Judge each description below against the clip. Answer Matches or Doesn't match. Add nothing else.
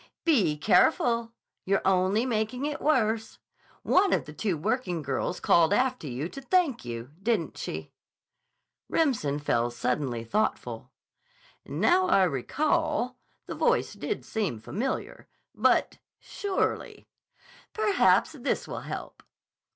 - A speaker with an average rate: Doesn't match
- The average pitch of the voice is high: Matches